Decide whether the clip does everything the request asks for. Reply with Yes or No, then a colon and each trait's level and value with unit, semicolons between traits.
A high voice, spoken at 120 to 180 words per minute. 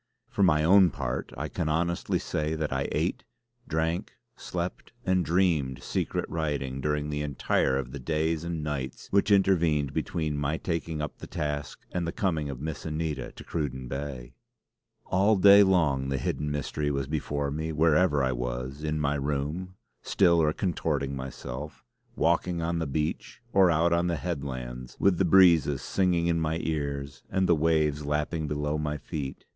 No: very low, 75 Hz; average, 170 wpm